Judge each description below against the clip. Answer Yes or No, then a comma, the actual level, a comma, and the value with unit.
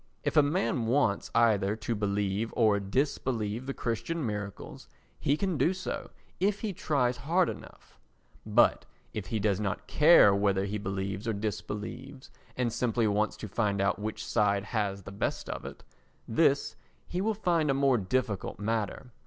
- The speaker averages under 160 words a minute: No, average, 165 wpm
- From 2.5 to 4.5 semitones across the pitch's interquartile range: No, average, 5.2 semitones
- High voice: No, low, 110 Hz